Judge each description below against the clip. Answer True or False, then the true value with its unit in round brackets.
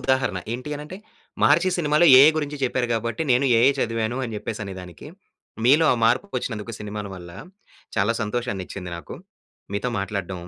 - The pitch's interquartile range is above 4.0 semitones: True (4.8 semitones)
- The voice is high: False (115 Hz)